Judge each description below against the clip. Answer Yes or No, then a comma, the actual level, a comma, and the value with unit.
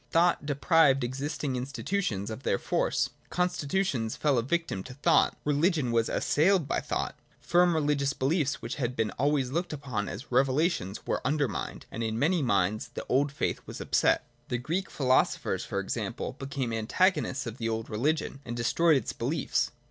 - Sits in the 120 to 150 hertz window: Yes, medium, 140 Hz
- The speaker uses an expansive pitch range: No, average, 4.9 semitones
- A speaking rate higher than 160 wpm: Yes, average, 170 wpm